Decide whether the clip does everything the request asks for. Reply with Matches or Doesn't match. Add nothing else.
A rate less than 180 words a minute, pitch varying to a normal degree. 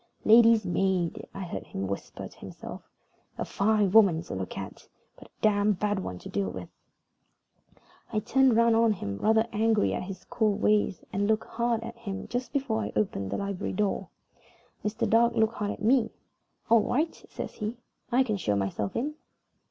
Doesn't match